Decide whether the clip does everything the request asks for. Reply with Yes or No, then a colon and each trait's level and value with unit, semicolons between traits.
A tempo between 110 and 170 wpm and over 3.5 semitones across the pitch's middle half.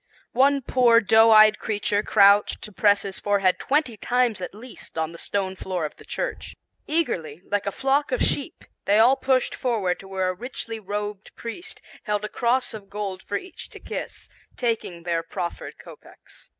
No: average, 180 wpm; average, 4.1 semitones